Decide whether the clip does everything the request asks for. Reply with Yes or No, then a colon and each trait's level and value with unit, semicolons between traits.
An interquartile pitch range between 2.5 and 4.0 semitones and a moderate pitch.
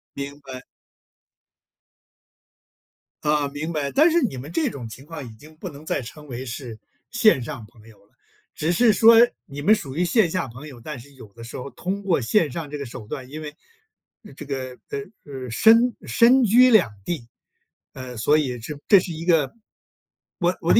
No: average, 5.3 semitones; medium, 145 Hz